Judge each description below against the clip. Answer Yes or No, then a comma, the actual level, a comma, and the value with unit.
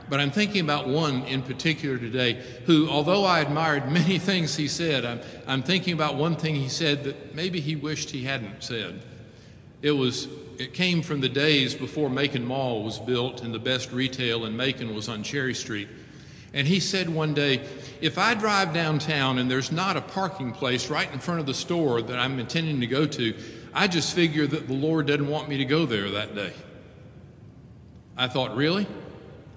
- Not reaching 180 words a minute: No, average, 195 wpm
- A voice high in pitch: No, medium, 140 Hz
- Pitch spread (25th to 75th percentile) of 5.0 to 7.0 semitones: No, average, 3.8 semitones